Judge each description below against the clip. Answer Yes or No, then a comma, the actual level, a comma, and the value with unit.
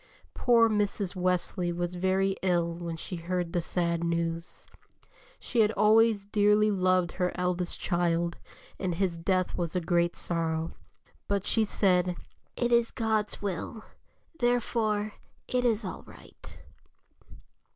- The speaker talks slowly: Yes, slow, 130 wpm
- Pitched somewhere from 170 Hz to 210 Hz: Yes, medium, 185 Hz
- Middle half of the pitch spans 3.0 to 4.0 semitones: Yes, average, 3.5 semitones